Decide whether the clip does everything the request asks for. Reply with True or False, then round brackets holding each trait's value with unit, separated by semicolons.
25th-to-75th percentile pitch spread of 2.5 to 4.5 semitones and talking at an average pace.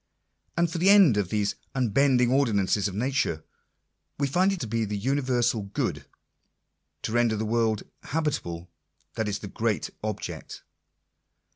False (4.9 semitones; 150 wpm)